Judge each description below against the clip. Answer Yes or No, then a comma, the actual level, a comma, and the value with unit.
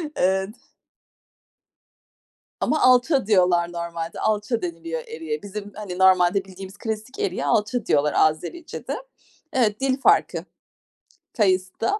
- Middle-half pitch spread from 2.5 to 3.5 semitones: No, average, 4.2 semitones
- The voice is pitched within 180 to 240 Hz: Yes, high, 190 Hz